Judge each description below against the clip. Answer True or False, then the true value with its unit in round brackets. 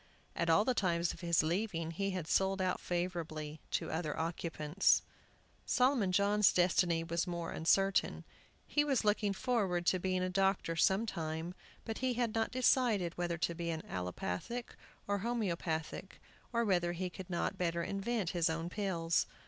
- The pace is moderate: True (160 wpm)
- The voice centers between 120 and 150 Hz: False (180 Hz)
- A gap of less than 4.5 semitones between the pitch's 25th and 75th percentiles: True (3.3 semitones)